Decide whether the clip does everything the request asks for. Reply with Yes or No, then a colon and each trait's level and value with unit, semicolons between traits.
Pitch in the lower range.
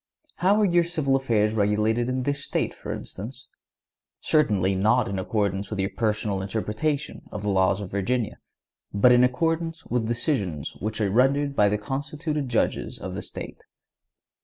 Yes: low, 115 Hz